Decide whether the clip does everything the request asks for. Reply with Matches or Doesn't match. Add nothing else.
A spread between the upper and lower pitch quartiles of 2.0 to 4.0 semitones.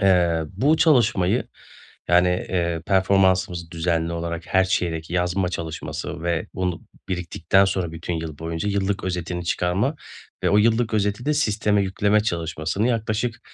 Matches